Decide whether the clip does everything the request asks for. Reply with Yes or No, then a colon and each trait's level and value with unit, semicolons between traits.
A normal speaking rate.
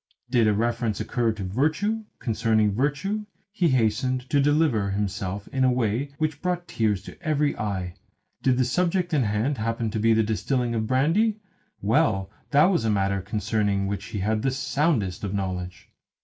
Yes: average, 175 wpm